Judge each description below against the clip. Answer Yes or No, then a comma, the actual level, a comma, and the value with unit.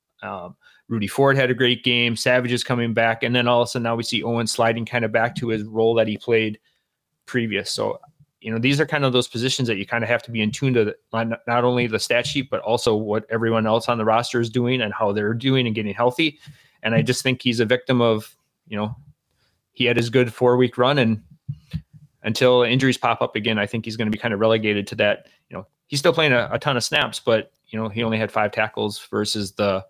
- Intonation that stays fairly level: Yes, narrow, 2.2 semitones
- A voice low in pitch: Yes, low, 120 Hz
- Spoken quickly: Yes, fast, 255 wpm